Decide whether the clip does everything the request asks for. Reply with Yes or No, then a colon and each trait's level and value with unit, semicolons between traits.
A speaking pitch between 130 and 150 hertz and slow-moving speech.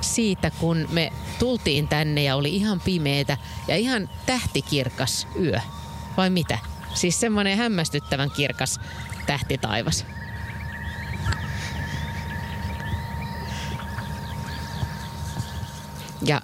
Yes: low, 135 Hz; slow, 80 wpm